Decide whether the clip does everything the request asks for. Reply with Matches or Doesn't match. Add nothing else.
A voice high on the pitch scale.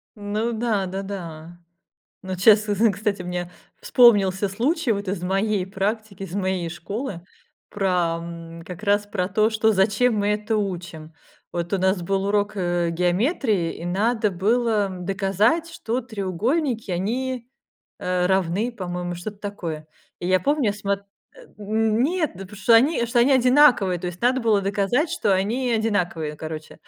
Matches